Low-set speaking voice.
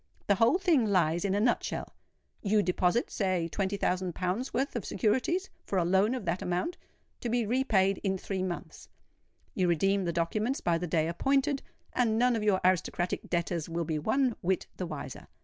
No: high, 195 Hz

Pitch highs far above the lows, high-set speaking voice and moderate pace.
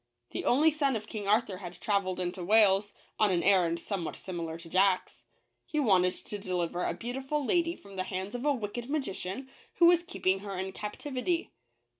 Yes: wide, 6.0 semitones; high, 200 Hz; average, 185 wpm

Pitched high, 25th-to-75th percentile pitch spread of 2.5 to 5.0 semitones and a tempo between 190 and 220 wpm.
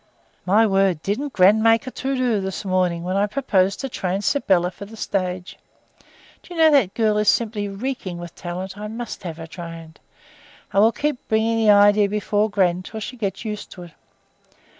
Yes: high, 205 Hz; average, 3.5 semitones; average, 195 wpm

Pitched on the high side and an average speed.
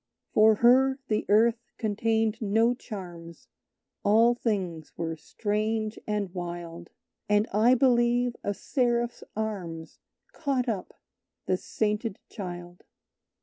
No: high, 215 Hz; slow, 105 wpm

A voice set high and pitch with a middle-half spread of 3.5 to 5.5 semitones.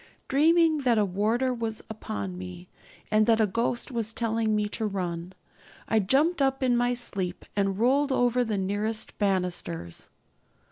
Yes: high, 220 Hz; average, 4.1 semitones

